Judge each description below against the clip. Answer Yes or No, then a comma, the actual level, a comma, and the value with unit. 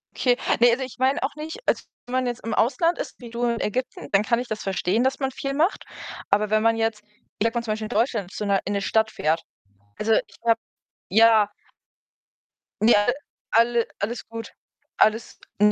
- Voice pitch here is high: Yes, high, 230 Hz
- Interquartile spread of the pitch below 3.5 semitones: Yes, narrow, 2.6 semitones